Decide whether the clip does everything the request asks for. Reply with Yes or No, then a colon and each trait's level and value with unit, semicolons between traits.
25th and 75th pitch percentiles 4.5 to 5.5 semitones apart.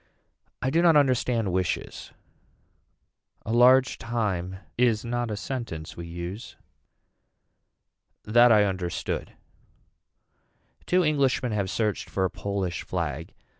Yes: average, 5.1 semitones